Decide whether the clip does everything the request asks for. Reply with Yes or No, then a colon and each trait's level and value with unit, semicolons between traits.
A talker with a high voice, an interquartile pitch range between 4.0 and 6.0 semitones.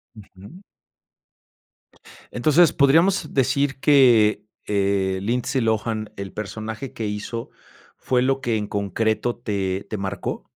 No: low, 110 Hz; average, 4.5 semitones